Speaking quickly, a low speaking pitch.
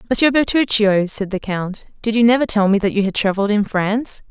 No: fast, 225 wpm; high, 210 Hz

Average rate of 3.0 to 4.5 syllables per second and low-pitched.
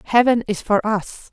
No: 4.4 syllables/s; high, 215 Hz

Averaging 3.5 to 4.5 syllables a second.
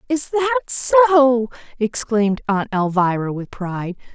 No: 4.9 syllables/s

